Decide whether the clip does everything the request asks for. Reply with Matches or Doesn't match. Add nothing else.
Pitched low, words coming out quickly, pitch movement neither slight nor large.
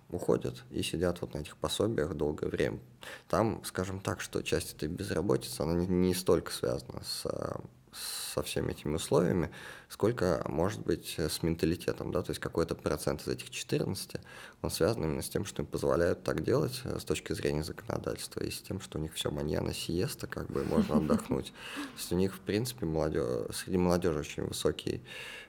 Matches